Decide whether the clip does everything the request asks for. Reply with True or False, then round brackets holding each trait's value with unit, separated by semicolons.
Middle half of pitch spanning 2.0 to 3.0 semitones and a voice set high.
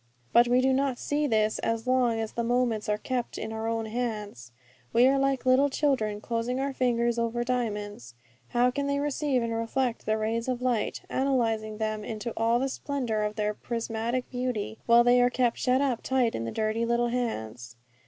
True (2.6 semitones; 235 Hz)